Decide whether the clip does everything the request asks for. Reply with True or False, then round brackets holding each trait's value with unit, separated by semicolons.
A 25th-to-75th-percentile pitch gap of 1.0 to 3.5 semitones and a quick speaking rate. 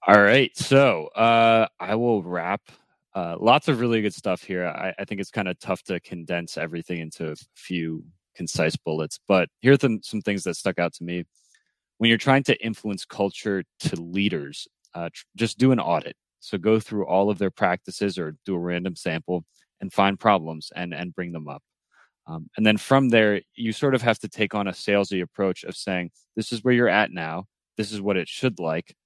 False (4.2 semitones; 215 wpm)